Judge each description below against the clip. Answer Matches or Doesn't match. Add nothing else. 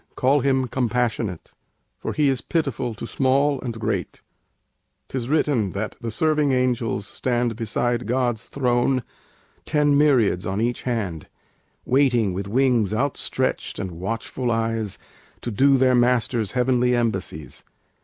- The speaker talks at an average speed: Doesn't match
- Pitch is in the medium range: Doesn't match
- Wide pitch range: Doesn't match